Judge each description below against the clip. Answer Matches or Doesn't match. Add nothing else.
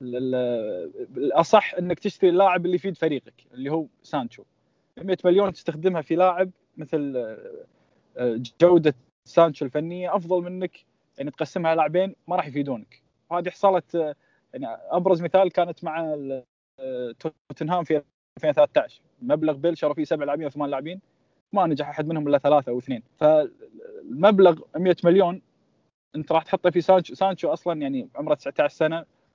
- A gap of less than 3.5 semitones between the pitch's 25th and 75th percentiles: Doesn't match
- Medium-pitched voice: Matches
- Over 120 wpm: Matches